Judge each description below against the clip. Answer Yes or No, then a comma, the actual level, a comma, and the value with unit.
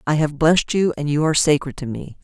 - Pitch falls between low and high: Yes, medium, 150 Hz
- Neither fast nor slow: No, fast, 270 wpm